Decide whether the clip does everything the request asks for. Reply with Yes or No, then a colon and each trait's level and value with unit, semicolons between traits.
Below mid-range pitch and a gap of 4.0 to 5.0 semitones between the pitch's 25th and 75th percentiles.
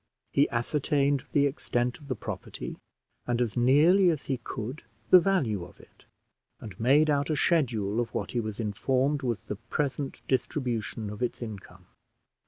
Yes: low, 125 Hz; average, 4.3 semitones